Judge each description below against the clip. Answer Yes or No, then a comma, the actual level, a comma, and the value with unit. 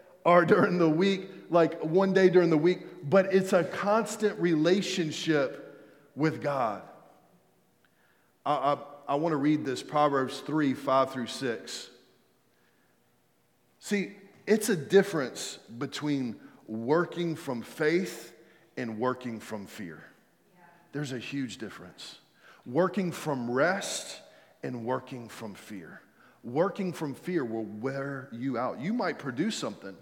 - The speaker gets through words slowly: Yes, slow, 125 wpm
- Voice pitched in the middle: Yes, medium, 155 Hz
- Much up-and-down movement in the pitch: Yes, wide, 5.7 semitones